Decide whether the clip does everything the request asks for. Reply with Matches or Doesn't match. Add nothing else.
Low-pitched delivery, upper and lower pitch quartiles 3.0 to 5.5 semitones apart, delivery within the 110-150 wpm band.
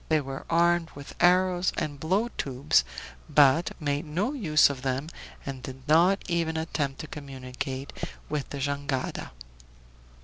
Doesn't match